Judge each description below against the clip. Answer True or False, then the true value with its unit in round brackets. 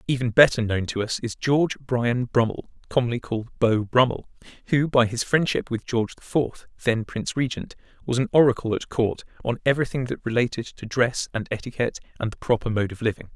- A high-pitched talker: False (120 Hz)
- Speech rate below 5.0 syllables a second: False (5.9 syllables/s)